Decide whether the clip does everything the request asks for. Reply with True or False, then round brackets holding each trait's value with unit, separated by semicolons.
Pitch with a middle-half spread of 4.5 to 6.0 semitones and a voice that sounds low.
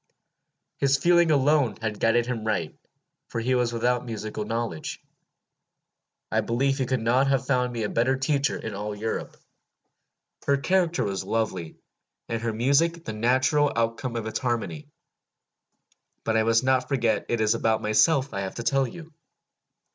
False (3.6 semitones; 120 Hz)